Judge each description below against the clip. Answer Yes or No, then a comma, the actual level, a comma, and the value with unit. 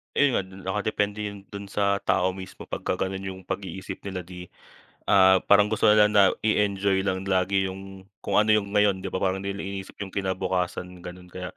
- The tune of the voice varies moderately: No, narrow, 1.4 semitones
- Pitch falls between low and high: No, very low, 95 Hz